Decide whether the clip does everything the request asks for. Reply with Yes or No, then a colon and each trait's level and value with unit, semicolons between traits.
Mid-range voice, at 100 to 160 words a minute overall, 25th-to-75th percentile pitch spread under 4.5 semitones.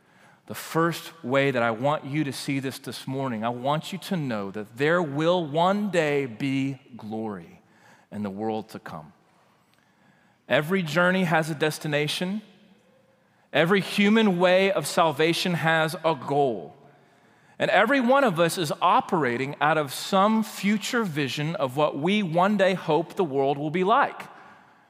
No: medium, 160 Hz; average, 155 wpm; average, 5.1 semitones